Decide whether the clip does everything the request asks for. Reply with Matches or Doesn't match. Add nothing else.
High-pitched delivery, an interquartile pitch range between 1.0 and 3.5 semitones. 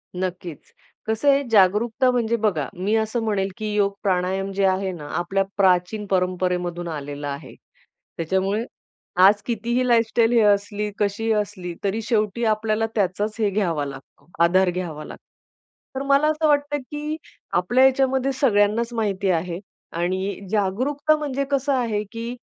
Doesn't match